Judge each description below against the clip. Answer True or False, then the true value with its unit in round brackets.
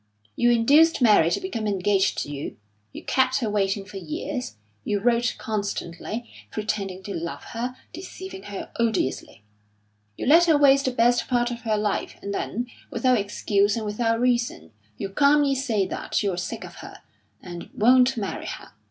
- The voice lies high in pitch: True (225 Hz)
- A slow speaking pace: False (170 wpm)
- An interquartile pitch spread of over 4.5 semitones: False (4.0 semitones)